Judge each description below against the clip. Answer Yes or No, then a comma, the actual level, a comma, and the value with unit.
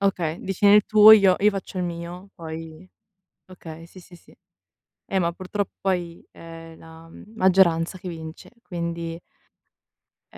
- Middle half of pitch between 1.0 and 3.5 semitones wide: Yes, narrow, 2.6 semitones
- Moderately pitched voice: Yes, medium, 175 Hz